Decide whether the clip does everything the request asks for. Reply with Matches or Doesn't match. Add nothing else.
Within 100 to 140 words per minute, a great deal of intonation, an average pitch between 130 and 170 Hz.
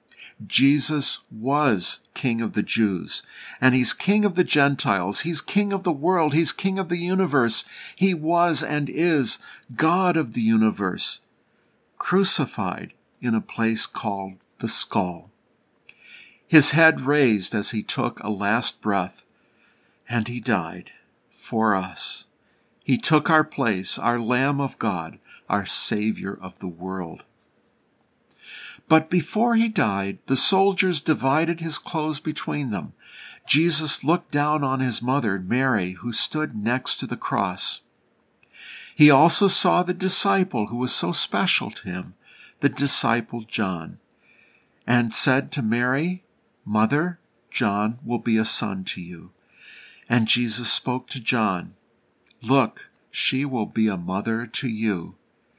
Matches